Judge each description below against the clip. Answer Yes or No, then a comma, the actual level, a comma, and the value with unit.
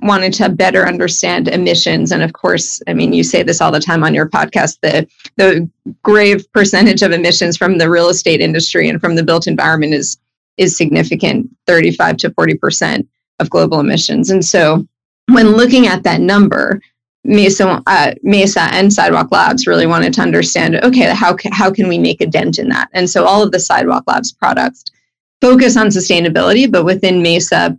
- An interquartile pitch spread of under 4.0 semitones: Yes, average, 3.4 semitones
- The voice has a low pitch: No, high, 190 Hz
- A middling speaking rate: Yes, average, 185 wpm